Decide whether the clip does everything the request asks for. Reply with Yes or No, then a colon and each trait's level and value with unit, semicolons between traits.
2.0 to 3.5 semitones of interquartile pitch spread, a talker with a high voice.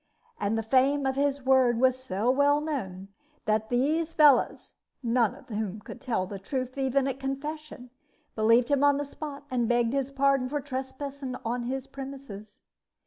Yes: average, 2.9 semitones; very high, 260 Hz